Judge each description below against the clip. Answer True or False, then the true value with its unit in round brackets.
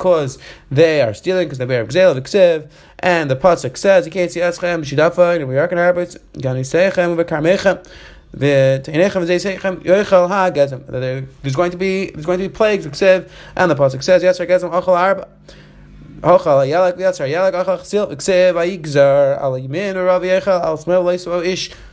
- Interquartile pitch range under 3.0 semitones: False (3.5 semitones)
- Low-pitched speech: False (175 Hz)